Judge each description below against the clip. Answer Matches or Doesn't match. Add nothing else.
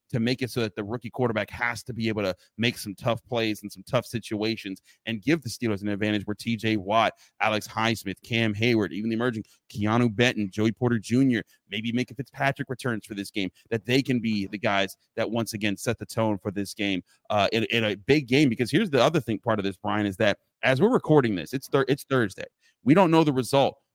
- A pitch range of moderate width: Matches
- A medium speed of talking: Doesn't match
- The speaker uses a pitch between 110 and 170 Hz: Matches